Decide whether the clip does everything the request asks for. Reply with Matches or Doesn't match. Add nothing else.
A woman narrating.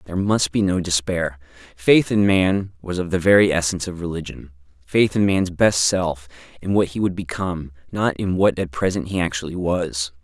Doesn't match